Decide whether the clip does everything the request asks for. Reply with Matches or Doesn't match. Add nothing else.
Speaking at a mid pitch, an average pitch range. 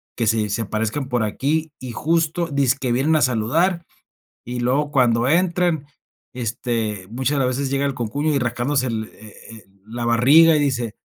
Doesn't match